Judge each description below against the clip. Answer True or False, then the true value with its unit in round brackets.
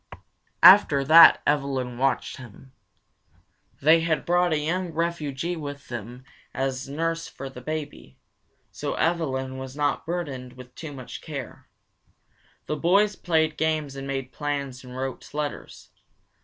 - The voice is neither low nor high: True (145 Hz)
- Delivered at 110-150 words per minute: True (135 wpm)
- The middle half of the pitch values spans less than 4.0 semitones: True (3.5 semitones)